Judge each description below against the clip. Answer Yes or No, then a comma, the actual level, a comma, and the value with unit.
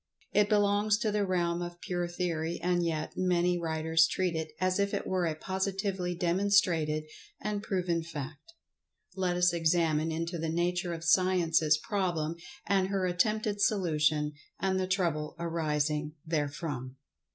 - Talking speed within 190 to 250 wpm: No, average, 145 wpm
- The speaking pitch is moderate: Yes, medium, 175 Hz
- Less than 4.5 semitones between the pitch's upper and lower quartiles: Yes, average, 2.8 semitones